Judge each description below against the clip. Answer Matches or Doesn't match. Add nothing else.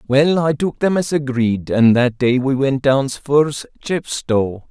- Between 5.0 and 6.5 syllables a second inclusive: Doesn't match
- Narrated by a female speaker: Doesn't match